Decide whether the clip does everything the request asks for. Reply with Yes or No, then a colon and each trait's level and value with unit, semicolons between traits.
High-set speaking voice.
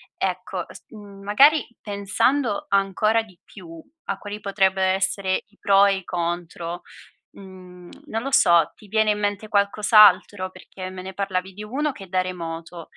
Yes: high, 195 Hz